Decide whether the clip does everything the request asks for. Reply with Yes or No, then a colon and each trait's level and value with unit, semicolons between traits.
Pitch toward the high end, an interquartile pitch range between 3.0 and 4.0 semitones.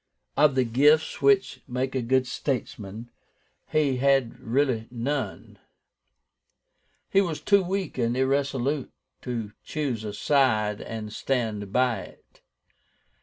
No: low, 130 Hz; average, 3.3 semitones